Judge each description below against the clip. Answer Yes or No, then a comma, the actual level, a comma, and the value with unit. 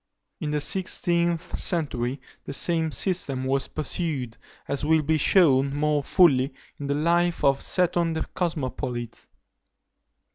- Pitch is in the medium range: Yes, medium, 150 Hz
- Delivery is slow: Yes, slow, 130 wpm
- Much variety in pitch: No, average, 3.8 semitones